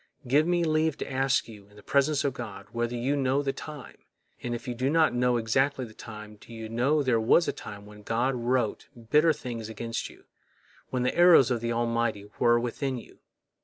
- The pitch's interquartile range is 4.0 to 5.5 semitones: No, average, 3.3 semitones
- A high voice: No, low, 120 Hz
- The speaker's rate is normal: No, fast, 210 wpm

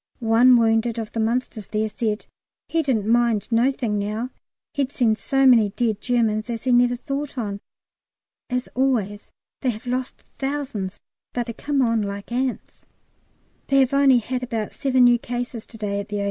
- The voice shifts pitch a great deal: No, average, 2.9 semitones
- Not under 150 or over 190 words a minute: Yes, average, 175 wpm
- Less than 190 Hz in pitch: No, high, 240 Hz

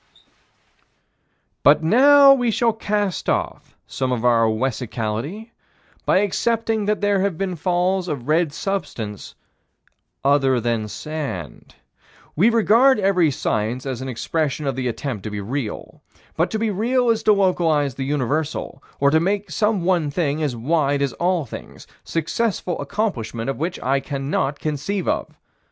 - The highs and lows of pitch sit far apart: Yes, wide, 7.0 semitones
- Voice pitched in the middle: Yes, medium, 155 Hz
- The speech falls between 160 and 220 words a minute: No, average, 150 wpm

